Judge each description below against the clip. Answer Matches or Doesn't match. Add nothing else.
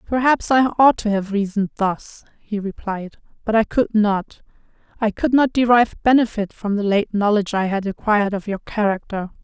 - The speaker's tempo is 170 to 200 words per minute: Matches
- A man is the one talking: Doesn't match